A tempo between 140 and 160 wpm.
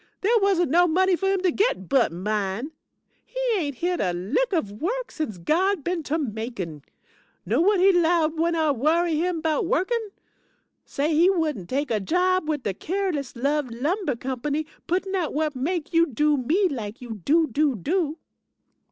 No: average, 180 wpm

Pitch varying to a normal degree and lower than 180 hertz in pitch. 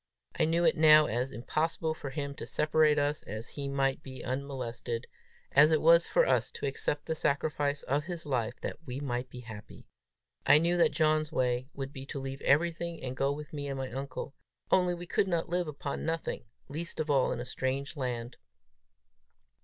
Yes: average, 3.1 semitones; medium, 140 Hz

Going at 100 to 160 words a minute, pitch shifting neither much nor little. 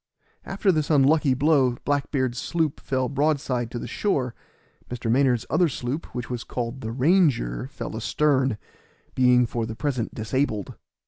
Yes: average, 150 wpm; average, 3.3 semitones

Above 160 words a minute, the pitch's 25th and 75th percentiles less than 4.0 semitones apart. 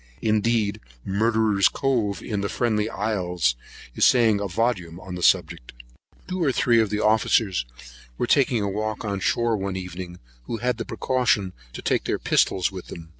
Yes: average, 175 wpm; average, 3.6 semitones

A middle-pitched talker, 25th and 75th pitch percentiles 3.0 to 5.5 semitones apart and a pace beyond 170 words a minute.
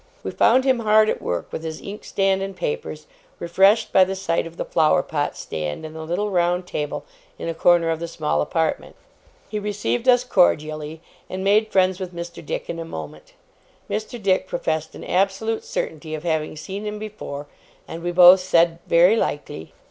Yes: medium, 175 Hz; average, 4.1 semitones; average, 185 wpm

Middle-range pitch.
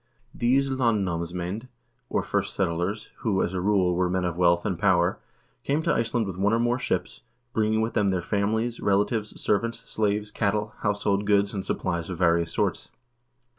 No: low, 100 Hz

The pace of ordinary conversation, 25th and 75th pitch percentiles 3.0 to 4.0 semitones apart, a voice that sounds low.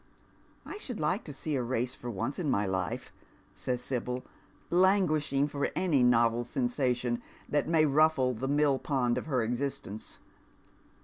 Yes: average, 160 wpm; average, 3.7 semitones; low, 130 Hz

